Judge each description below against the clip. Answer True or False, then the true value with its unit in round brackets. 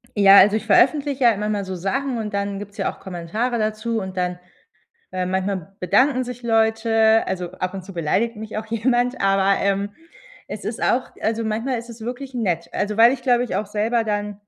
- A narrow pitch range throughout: False (3.1 semitones)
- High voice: True (215 Hz)